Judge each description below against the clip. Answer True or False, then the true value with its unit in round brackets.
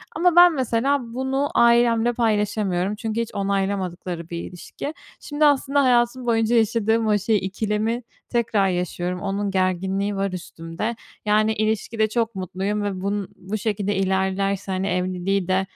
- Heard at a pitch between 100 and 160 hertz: False (205 Hz)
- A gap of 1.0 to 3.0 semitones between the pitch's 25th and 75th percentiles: False (3.4 semitones)